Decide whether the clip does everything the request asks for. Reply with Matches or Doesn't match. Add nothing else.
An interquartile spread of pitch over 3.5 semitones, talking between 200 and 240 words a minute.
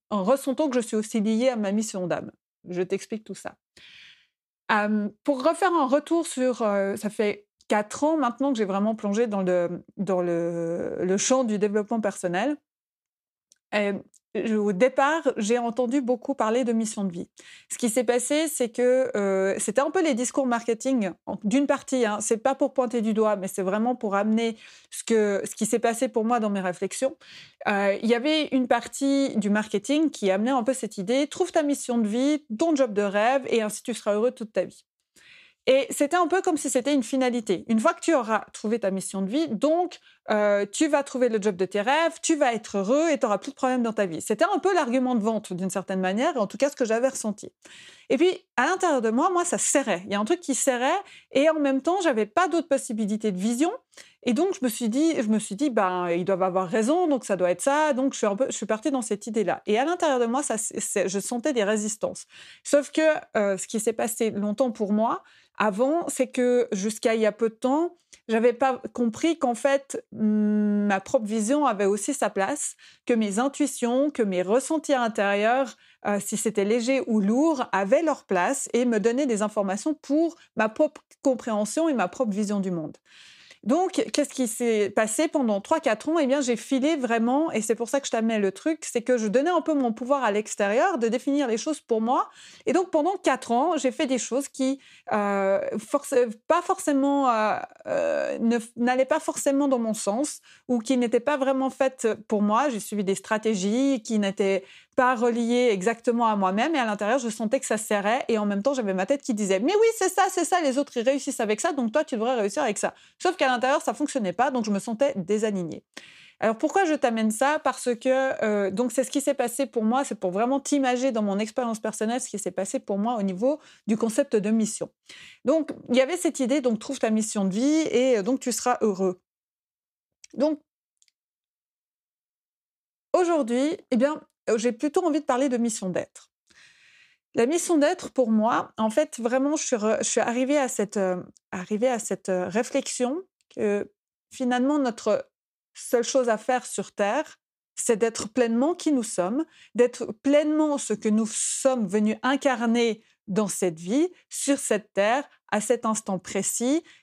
Matches